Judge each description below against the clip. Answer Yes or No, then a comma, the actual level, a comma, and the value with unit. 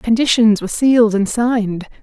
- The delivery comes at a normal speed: Yes, average, 150 wpm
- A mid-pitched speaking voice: No, high, 225 Hz